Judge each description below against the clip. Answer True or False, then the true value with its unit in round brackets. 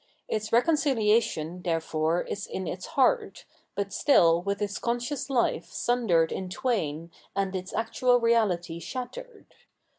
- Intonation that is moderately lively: False (5.9 semitones)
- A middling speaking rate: False (125 wpm)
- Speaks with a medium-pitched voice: False (205 Hz)